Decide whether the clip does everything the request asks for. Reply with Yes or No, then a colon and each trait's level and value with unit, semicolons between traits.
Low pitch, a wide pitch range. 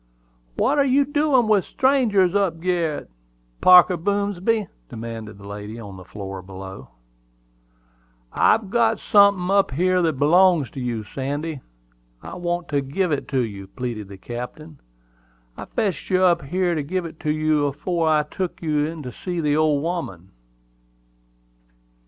No: medium, 160 Hz; wide, 6.3 semitones